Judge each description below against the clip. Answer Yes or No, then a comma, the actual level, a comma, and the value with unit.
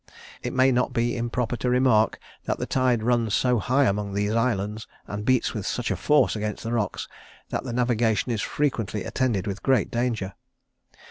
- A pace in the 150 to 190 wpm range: Yes, average, 180 wpm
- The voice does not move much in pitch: No, average, 3.0 semitones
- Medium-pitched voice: No, low, 115 Hz